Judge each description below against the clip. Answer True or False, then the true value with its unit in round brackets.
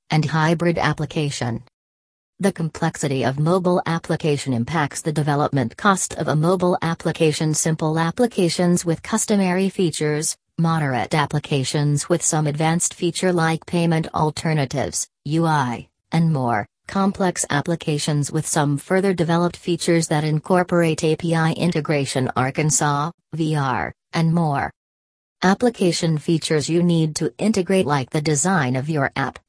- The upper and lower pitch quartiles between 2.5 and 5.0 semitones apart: True (2.8 semitones)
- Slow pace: True (120 wpm)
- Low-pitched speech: False (160 Hz)